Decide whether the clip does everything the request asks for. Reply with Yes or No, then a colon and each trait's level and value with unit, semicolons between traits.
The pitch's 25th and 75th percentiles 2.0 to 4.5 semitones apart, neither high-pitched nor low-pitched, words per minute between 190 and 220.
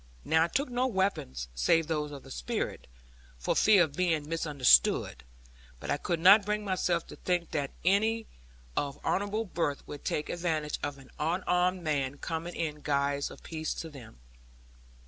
No: average, 4.1 semitones; medium, 160 Hz; average, 165 wpm